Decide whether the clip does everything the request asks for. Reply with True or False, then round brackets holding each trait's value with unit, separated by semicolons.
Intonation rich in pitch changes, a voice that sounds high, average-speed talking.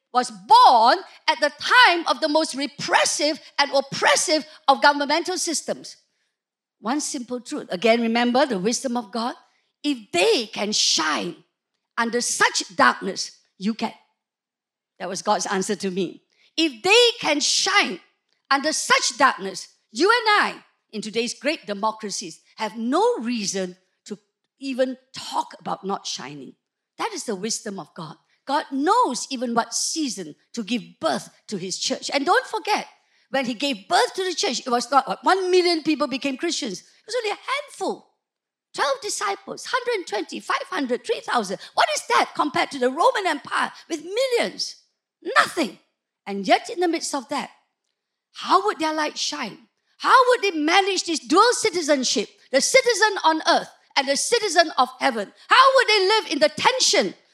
True (8.2 semitones; 295 Hz; 160 wpm)